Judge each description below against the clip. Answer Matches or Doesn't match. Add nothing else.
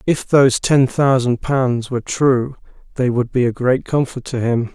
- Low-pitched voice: Matches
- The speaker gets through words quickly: Doesn't match